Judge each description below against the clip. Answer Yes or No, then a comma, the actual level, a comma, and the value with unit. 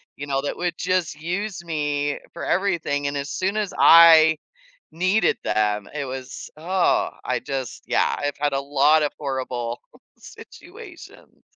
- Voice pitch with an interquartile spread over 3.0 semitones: Yes, average, 3.9 semitones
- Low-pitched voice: No, medium, 150 Hz